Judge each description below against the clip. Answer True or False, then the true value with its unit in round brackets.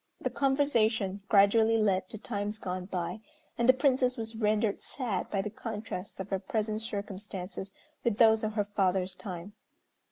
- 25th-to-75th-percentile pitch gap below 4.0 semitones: True (2.6 semitones)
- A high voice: True (210 Hz)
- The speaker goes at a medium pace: True (160 wpm)